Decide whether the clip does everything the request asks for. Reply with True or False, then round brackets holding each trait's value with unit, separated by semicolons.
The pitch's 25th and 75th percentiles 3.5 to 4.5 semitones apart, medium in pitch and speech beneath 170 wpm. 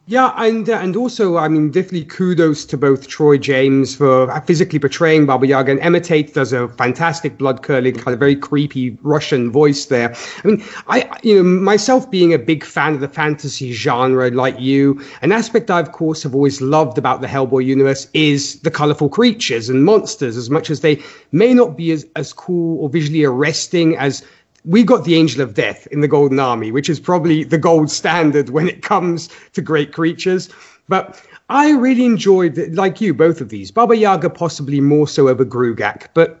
False (4.2 semitones; 155 Hz; 195 wpm)